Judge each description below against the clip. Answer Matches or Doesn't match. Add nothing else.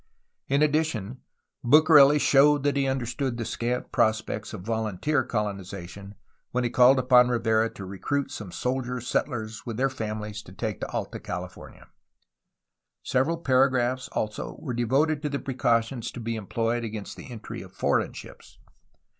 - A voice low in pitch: Matches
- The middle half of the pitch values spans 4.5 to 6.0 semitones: Doesn't match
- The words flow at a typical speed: Matches